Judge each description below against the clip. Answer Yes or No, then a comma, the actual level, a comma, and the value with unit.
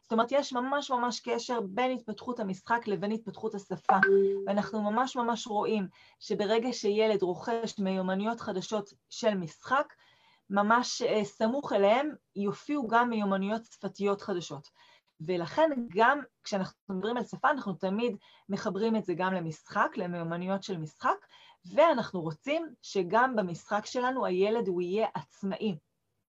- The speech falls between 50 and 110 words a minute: No, average, 130 wpm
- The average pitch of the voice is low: No, high, 210 Hz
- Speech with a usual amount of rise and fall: Yes, average, 3.6 semitones